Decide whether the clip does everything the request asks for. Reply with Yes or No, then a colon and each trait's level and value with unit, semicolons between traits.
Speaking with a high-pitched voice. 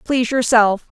Yes: high, 235 Hz